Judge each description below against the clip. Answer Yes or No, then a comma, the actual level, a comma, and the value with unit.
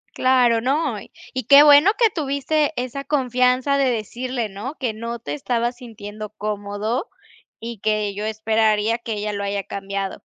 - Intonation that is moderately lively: Yes, average, 3.6 semitones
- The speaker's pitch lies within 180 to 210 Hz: No, high, 230 Hz